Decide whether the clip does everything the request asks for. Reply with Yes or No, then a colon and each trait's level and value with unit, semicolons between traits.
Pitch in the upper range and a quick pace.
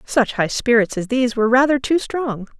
Yes: high, 245 Hz; fast, 210 wpm